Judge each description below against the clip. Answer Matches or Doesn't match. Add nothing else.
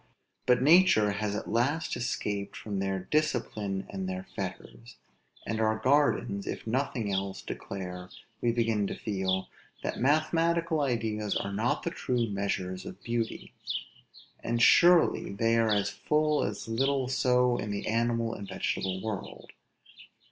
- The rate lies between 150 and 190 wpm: Doesn't match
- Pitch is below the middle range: Matches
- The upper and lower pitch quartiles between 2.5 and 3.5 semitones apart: Doesn't match